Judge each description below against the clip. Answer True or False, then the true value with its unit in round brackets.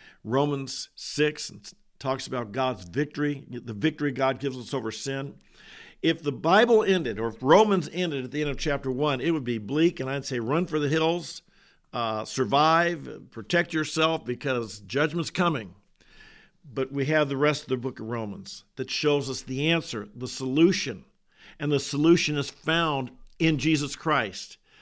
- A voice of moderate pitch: True (145 Hz)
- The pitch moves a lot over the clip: False (3.5 semitones)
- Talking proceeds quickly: False (170 wpm)